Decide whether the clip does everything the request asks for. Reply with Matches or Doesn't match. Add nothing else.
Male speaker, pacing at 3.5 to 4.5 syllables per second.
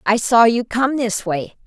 Doesn't match